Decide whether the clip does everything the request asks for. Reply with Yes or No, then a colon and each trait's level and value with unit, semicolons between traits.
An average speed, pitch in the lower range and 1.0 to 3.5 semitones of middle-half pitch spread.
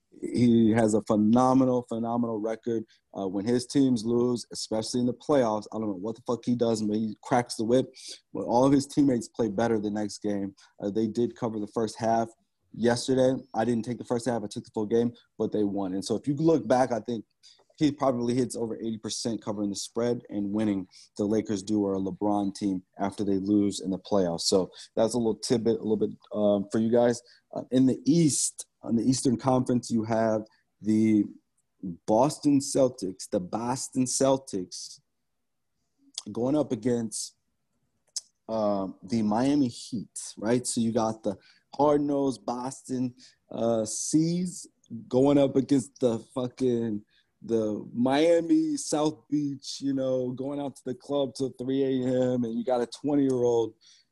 Yes: average, 180 wpm; low, 120 Hz; average, 3.1 semitones